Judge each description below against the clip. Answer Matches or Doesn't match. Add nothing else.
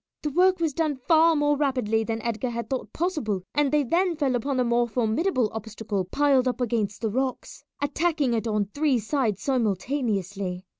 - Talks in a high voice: Matches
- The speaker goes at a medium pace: Matches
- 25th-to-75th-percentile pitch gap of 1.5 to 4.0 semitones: Doesn't match